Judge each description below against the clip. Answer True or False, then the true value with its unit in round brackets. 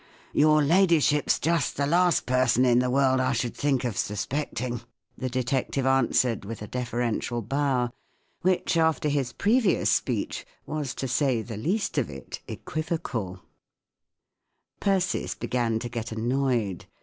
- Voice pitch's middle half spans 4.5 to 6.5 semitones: False (4.1 semitones)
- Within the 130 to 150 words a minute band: True (135 wpm)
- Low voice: True (130 Hz)